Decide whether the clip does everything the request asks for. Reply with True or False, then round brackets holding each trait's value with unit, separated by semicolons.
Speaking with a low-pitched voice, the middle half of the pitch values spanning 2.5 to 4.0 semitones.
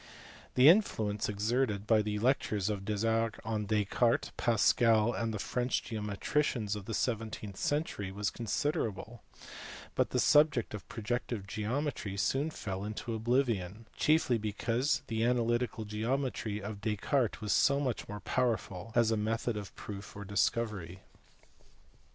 True (110 Hz; 2.8 semitones)